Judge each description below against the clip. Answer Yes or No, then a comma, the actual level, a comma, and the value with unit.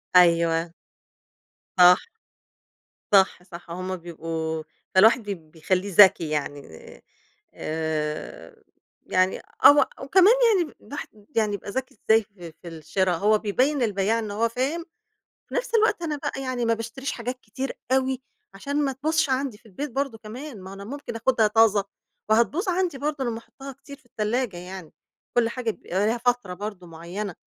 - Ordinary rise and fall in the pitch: No, wide, 6.4 semitones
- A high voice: Yes, high, 220 Hz